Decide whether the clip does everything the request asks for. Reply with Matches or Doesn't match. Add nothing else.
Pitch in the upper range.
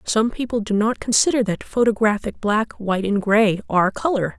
Matches